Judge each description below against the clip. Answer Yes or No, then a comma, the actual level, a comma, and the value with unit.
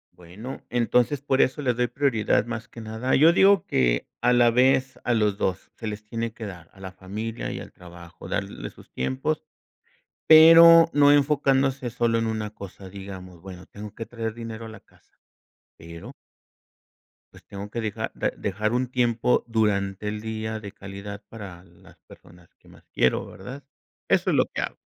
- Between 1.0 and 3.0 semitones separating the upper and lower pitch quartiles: No, average, 4.1 semitones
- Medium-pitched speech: No, low, 110 Hz